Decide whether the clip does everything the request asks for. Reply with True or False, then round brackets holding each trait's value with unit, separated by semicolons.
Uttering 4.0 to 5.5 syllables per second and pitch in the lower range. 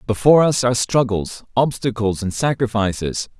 True (5.2 syllables/s; 115 Hz)